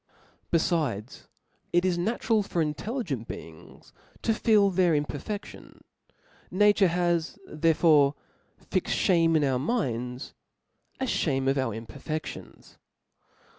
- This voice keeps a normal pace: No, slow, 105 wpm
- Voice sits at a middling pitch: Yes, medium, 165 Hz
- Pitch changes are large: Yes, wide, 5.8 semitones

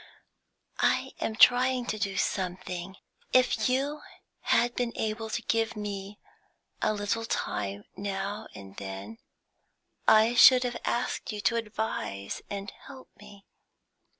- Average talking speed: No, slow, 125 wpm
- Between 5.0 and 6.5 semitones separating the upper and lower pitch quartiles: No, average, 3.6 semitones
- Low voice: No, high, 210 Hz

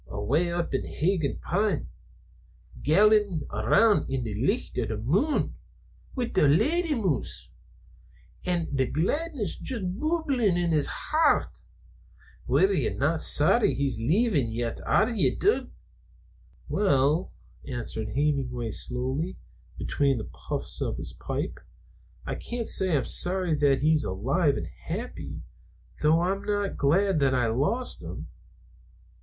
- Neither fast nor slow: No, slow, 130 wpm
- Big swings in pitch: Yes, wide, 7.8 semitones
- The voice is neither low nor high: Yes, medium, 160 Hz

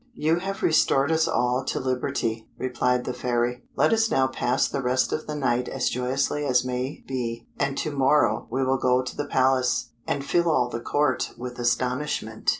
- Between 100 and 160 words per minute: No, average, 190 wpm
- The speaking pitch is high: No, low, 130 Hz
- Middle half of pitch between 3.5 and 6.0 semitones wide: No, narrow, 2.4 semitones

